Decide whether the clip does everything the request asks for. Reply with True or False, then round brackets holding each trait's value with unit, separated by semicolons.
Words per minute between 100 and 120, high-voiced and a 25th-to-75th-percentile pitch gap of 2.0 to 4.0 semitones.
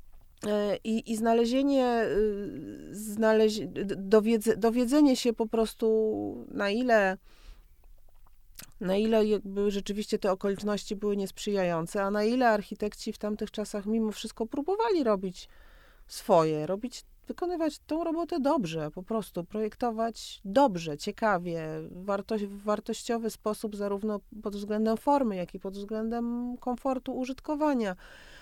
True (115 wpm; 215 Hz; 2.7 semitones)